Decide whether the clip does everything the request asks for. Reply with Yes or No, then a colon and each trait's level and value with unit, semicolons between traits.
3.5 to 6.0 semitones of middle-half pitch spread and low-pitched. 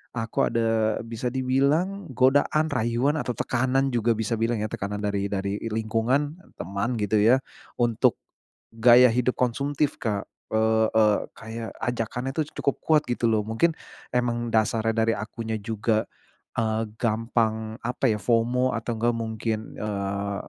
No: narrow, 2.4 semitones; low, 115 Hz